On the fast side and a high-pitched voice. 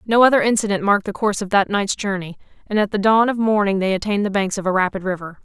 Yes: fast, 265 wpm; high, 200 Hz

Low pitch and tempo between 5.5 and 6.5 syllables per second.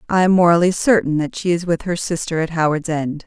No: medium, 165 Hz; 5.8 syllables/s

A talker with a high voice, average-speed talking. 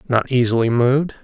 No: low, 125 Hz; average, 145 wpm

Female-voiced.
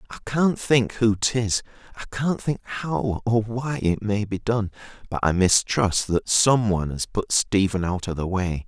No: male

